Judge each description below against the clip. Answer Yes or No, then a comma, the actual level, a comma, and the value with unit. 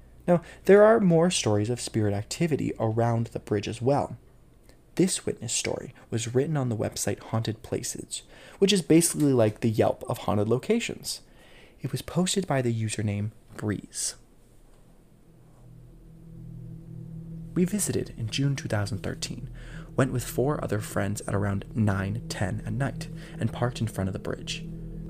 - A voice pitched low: Yes, low, 125 Hz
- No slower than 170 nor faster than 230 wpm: No, average, 145 wpm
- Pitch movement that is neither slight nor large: No, wide, 6.6 semitones